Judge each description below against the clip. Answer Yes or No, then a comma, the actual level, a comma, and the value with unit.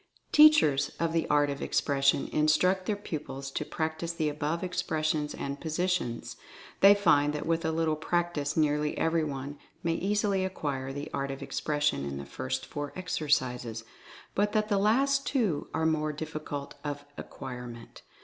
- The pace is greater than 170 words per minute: No, average, 160 wpm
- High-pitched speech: No, medium, 155 Hz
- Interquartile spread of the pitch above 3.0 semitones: Yes, average, 4.0 semitones